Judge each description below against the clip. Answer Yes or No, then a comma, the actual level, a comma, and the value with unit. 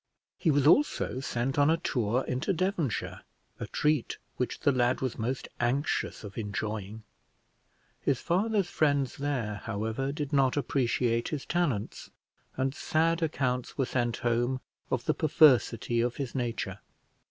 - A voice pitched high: No, low, 130 Hz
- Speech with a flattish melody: No, average, 3.8 semitones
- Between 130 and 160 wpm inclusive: Yes, average, 140 wpm